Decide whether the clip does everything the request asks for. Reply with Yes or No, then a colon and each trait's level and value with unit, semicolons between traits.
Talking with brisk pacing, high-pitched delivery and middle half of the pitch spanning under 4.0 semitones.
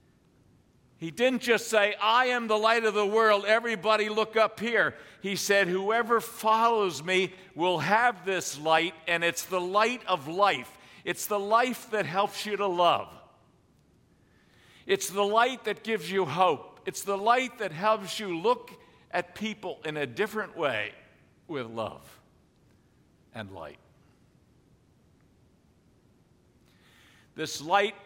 No: slow, 135 wpm; high, 205 Hz; average, 3.3 semitones